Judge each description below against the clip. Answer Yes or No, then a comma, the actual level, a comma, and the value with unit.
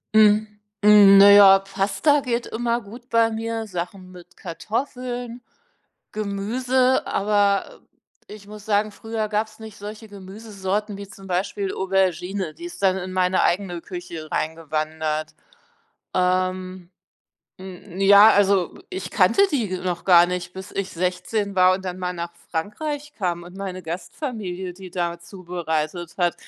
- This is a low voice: No, high, 195 Hz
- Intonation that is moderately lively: Yes, average, 3.0 semitones